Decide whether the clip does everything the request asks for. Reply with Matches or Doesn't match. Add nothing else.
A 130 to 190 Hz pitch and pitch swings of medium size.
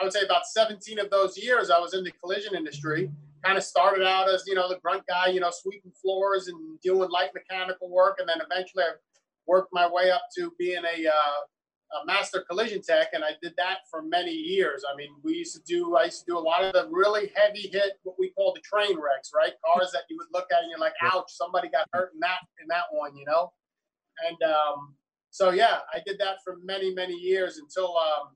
Matches